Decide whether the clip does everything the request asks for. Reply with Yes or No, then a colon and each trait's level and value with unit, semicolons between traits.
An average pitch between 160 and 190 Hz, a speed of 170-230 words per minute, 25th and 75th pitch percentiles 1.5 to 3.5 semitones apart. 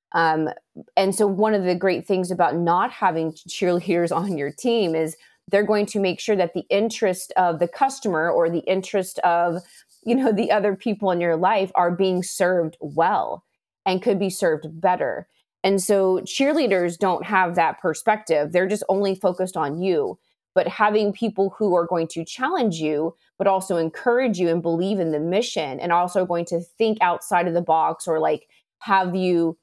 Yes: medium, 185 Hz; average, 185 wpm; average, 3.0 semitones